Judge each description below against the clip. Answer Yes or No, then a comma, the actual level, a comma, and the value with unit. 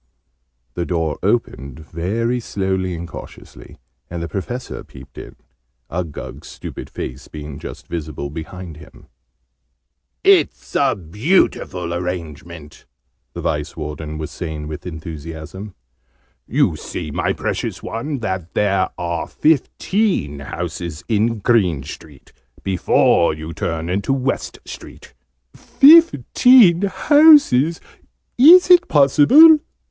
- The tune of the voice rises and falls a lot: Yes, wide, 8.3 semitones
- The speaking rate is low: Yes, slow, 110 wpm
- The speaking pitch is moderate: No, very low, 90 Hz